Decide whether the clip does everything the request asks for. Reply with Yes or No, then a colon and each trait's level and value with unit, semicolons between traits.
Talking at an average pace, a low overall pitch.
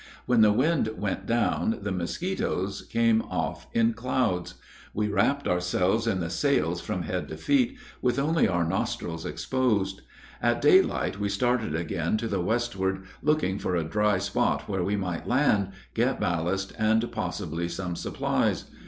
Yes: average, 155 wpm; low, 100 Hz